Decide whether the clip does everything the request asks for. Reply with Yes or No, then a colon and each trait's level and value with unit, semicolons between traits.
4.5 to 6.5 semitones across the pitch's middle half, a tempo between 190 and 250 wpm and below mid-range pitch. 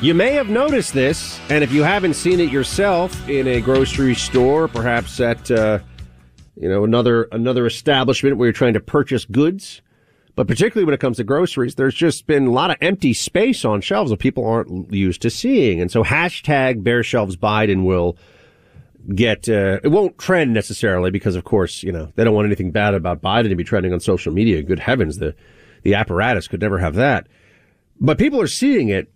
Yes: average, 5.3 semitones; average, 200 wpm; low, 120 Hz